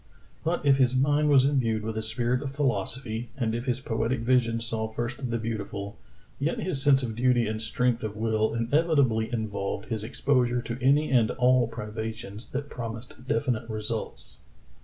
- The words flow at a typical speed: Yes, average, 170 wpm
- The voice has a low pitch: Yes, low, 120 Hz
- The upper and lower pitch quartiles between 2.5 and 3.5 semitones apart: Yes, average, 3.0 semitones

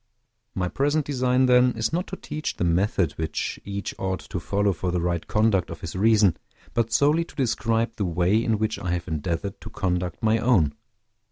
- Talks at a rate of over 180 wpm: Yes, average, 195 wpm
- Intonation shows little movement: No, average, 5.0 semitones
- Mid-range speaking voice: No, low, 100 Hz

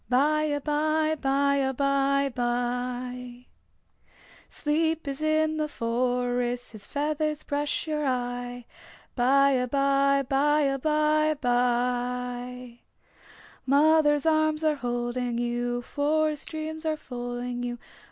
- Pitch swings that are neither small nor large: Yes, average, 3.7 semitones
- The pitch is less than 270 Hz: No, very high, 275 Hz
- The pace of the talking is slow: Yes, slow, 100 wpm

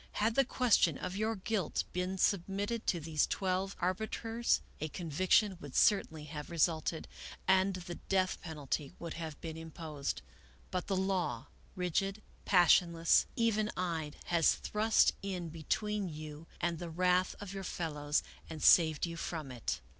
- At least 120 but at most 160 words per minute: Yes, average, 150 wpm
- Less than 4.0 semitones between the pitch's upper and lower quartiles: Yes, average, 3.5 semitones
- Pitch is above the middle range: No, medium, 175 Hz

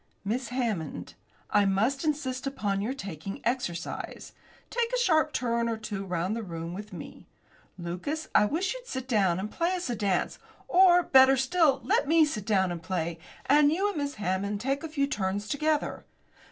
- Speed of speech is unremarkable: Yes, average, 180 wpm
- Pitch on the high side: Yes, high, 235 Hz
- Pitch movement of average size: No, wide, 7.2 semitones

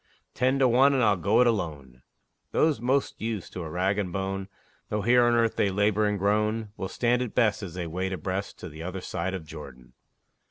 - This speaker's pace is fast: Yes, fast, 215 wpm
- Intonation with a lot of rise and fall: No, average, 4.1 semitones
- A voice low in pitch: Yes, low, 100 Hz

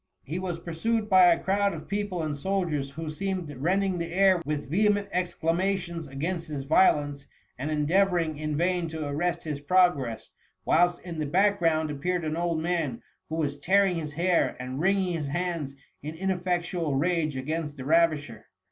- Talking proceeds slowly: No, average, 175 wpm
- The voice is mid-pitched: Yes, medium, 165 Hz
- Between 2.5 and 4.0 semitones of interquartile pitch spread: Yes, average, 3.5 semitones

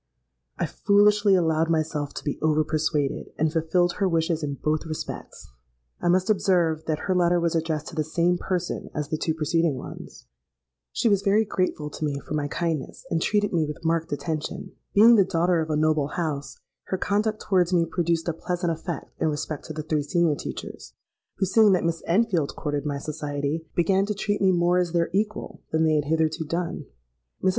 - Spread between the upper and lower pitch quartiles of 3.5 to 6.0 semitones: No, average, 2.9 semitones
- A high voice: No, medium, 165 Hz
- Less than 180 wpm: No, average, 200 wpm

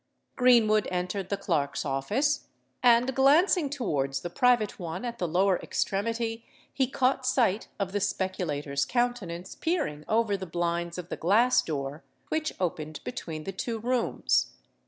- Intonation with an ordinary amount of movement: No, wide, 6.2 semitones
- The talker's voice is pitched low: No, high, 200 Hz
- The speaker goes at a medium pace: Yes, average, 145 wpm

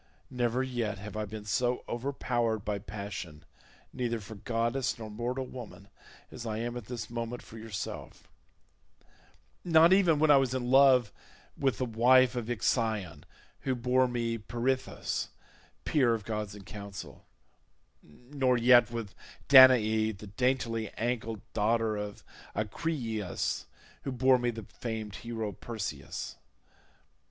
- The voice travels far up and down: No, average, 2.9 semitones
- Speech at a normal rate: No, slow, 130 wpm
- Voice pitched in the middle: No, low, 115 Hz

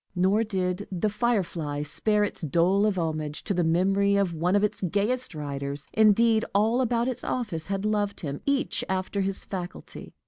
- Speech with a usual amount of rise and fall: Yes, average, 3.9 semitones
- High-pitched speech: Yes, high, 195 Hz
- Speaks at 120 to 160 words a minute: No, average, 175 wpm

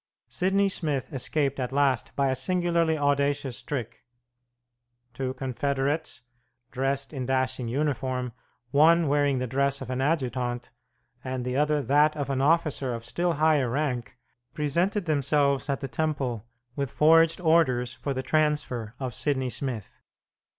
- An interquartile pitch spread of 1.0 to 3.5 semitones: Yes, average, 2.9 semitones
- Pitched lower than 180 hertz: Yes, medium, 140 Hz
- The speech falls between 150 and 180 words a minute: No, average, 140 wpm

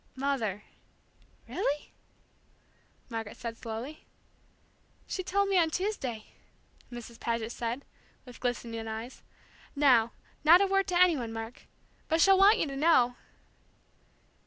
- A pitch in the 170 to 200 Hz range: No, very high, 255 Hz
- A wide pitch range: Yes, wide, 7.0 semitones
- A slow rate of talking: Yes, slow, 125 wpm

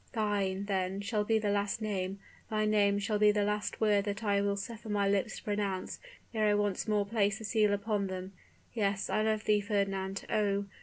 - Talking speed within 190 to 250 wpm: Yes, fast, 205 wpm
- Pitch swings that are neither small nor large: No, narrow, 1.2 semitones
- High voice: Yes, high, 205 Hz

